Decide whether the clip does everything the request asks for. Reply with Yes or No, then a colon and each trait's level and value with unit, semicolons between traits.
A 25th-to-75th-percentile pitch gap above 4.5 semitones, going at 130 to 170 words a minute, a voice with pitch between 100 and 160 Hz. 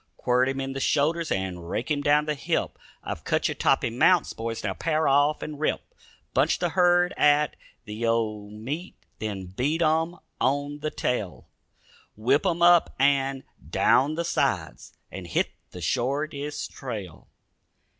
Yes: average, 5.1 semitones; average, 155 wpm; medium, 140 Hz